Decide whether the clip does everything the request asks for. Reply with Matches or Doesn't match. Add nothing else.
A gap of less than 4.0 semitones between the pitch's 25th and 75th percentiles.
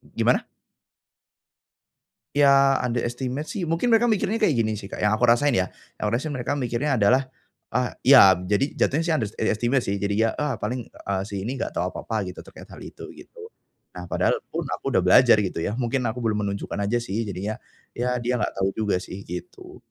Doesn't match